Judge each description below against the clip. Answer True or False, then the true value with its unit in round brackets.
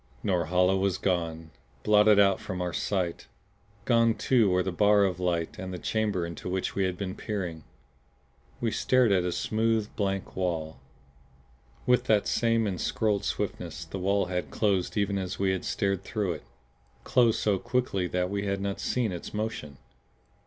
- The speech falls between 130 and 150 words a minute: False (165 wpm)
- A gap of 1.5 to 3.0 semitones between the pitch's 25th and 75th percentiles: True (2.7 semitones)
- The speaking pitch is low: True (95 Hz)